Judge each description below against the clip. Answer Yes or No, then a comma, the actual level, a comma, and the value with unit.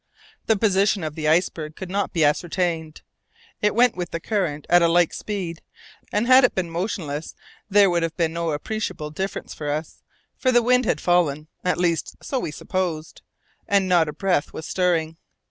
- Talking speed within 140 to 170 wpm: No, average, 185 wpm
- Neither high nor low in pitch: Yes, medium, 175 Hz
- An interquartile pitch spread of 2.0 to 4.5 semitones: Yes, average, 4.0 semitones